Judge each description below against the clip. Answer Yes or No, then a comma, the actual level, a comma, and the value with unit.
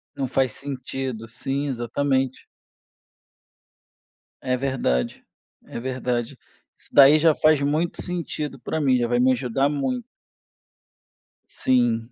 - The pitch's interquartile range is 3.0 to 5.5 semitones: No, narrow, 2.6 semitones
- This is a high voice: No, low, 130 Hz